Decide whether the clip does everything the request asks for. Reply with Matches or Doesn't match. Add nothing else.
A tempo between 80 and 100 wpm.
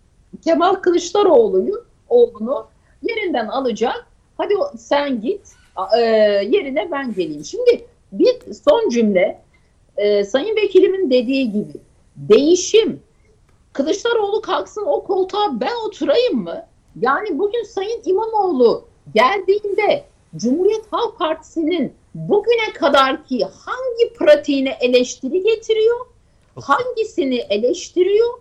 Matches